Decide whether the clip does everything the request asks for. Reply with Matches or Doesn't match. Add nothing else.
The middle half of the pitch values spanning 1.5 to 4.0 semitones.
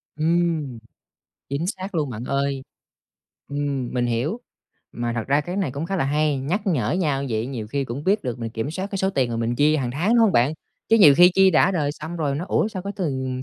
Doesn't match